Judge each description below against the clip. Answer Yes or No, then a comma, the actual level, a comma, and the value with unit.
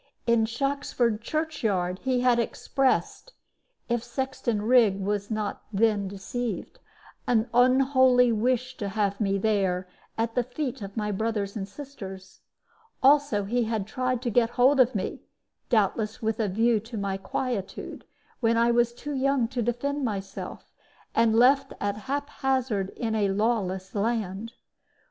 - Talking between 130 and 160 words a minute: Yes, average, 145 wpm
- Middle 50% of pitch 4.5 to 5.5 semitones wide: No, average, 3.7 semitones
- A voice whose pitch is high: Yes, high, 230 Hz